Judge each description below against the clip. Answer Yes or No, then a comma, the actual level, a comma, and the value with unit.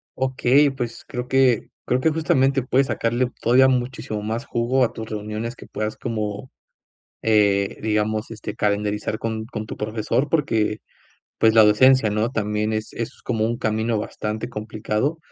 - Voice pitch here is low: Yes, low, 110 Hz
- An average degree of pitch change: Yes, average, 3.0 semitones